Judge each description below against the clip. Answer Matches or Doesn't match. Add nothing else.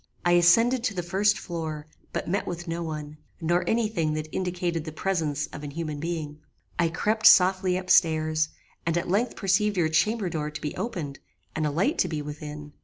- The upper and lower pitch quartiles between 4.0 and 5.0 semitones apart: Doesn't match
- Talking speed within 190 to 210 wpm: Matches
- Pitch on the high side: Doesn't match